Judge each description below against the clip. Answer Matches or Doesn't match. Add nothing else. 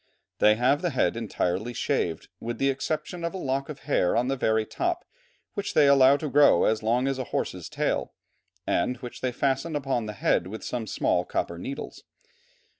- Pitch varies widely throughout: Doesn't match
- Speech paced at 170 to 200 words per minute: Matches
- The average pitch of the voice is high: Doesn't match